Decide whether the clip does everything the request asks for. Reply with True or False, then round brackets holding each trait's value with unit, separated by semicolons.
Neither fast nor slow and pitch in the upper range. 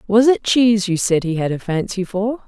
False (245 wpm; 205 Hz)